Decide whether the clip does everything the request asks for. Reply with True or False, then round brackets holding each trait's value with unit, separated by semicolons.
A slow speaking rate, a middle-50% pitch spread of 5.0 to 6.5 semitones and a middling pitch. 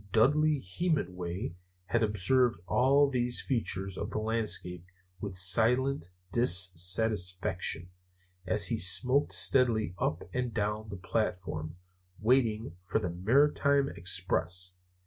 False (110 wpm; 5.4 semitones; 105 Hz)